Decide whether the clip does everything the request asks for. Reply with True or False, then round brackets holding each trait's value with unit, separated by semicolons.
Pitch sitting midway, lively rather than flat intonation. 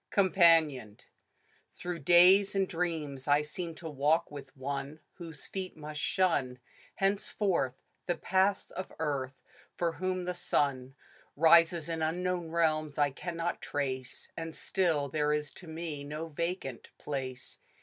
False (160 Hz; 3.6 semitones)